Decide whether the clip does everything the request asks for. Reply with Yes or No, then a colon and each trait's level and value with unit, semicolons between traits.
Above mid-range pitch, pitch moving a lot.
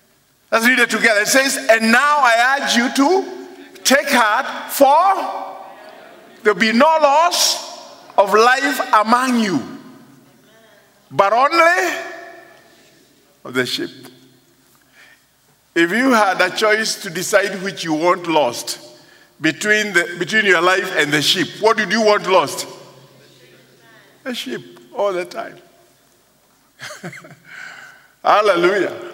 Yes: very high, 250 Hz; wide, 7.7 semitones